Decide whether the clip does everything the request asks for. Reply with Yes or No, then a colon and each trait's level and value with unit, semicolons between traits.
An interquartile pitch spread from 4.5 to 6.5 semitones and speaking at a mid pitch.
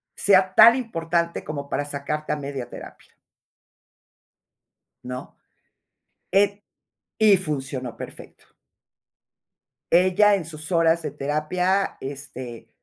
Yes: average, 4.9 semitones; medium, 160 Hz